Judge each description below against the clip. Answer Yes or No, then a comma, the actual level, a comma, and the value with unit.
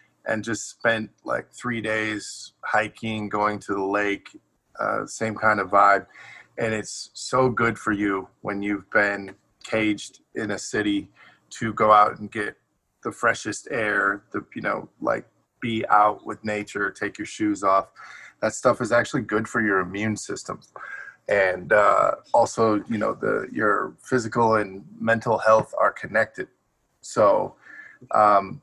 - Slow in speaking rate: No, average, 155 wpm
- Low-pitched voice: Yes, low, 105 Hz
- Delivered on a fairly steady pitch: Yes, narrow, 1.5 semitones